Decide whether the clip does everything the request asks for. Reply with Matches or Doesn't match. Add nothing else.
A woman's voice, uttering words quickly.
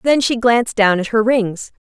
Matches